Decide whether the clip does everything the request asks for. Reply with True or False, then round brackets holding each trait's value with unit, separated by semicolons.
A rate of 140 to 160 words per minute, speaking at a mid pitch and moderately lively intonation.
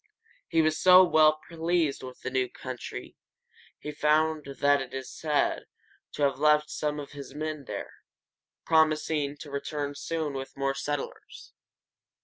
False (145 wpm; 150 Hz; 1.9 semitones)